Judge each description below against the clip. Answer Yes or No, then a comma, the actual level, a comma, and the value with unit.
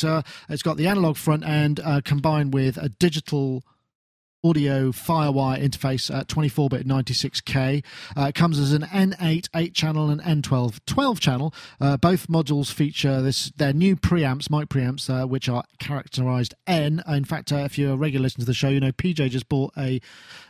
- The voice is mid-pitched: Yes, medium, 145 Hz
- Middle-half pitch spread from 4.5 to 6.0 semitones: No, average, 2.8 semitones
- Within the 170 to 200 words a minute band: Yes, average, 180 wpm